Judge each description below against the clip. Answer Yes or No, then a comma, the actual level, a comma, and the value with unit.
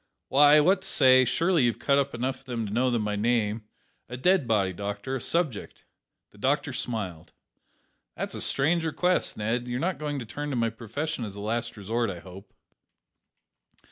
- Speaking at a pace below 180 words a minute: No, average, 190 wpm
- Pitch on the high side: No, low, 120 Hz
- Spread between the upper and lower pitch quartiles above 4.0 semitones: Yes, average, 5.2 semitones